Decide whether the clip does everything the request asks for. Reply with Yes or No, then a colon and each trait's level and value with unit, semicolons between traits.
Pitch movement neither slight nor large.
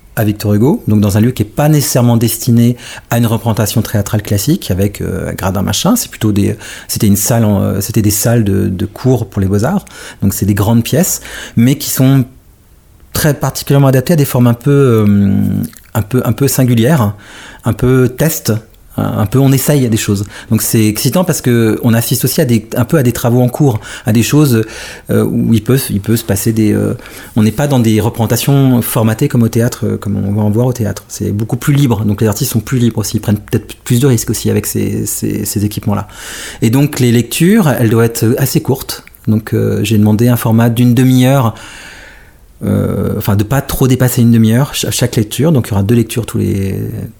Yes: average, 3.3 semitones